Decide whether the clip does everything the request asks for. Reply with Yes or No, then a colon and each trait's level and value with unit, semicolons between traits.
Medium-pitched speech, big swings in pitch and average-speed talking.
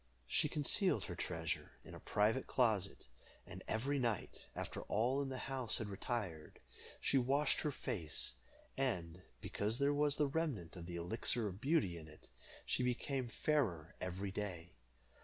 No: low, 110 Hz; wide, 7.3 semitones; average, 160 wpm